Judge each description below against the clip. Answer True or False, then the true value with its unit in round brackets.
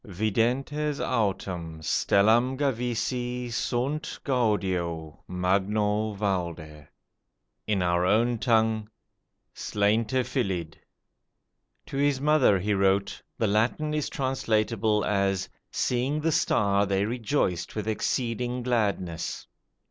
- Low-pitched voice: True (110 Hz)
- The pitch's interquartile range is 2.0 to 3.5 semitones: False (4.2 semitones)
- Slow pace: True (95 wpm)